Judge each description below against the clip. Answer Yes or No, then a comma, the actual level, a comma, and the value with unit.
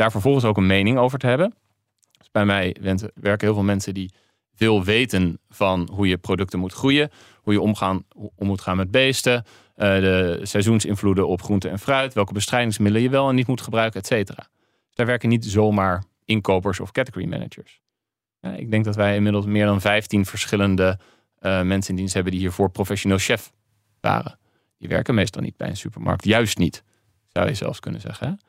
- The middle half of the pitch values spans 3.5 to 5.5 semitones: No, average, 2.7 semitones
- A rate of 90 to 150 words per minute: No, average, 195 wpm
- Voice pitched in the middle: No, low, 105 Hz